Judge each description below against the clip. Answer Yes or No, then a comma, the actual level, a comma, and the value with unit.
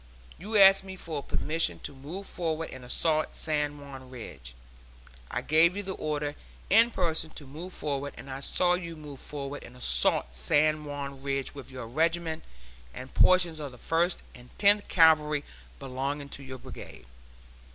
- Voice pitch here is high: No, medium, 150 Hz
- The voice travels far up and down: No, average, 3.6 semitones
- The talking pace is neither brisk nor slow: Yes, average, 165 wpm